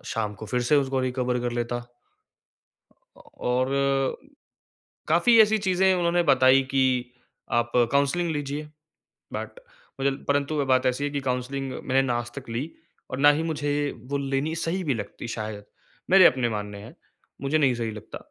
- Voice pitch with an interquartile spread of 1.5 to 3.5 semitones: Yes, average, 3.1 semitones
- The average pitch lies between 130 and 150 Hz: Yes, low, 135 Hz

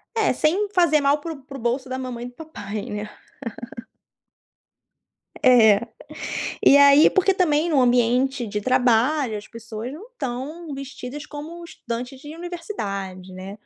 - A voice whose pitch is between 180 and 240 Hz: No, very high, 260 Hz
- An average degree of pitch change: Yes, average, 4.9 semitones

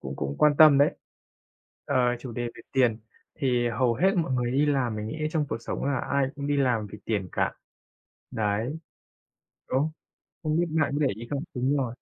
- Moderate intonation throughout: Yes, average, 3.9 semitones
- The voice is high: No, low, 130 Hz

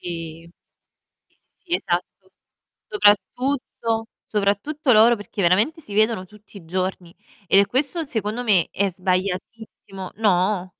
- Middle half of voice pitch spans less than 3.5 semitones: No, average, 3.8 semitones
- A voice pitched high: Yes, high, 205 Hz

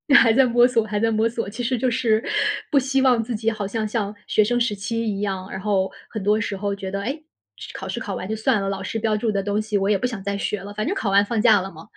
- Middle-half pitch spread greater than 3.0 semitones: No, narrow, 2.5 semitones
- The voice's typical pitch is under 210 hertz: No, high, 215 Hz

